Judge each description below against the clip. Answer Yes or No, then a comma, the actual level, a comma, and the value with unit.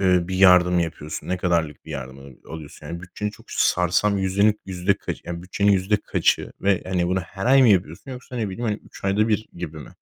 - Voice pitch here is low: Yes, very low, 90 Hz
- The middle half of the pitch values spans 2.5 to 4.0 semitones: Yes, average, 2.9 semitones